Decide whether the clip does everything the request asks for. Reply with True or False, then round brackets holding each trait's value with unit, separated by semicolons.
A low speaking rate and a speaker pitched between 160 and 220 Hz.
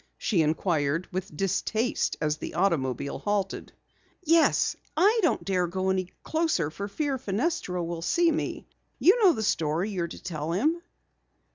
False (150 wpm; 190 Hz)